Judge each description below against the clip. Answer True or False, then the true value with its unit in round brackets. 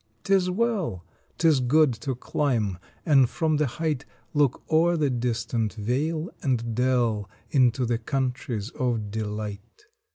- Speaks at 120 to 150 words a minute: True (140 wpm)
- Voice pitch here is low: True (125 Hz)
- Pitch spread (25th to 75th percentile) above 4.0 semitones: True (5.2 semitones)